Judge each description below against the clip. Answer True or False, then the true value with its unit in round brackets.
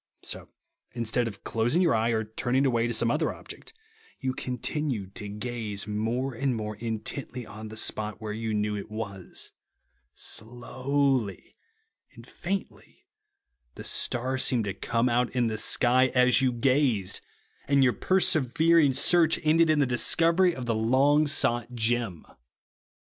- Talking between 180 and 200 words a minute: False (150 wpm)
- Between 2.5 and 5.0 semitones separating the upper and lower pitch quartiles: True (3.8 semitones)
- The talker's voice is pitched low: True (120 Hz)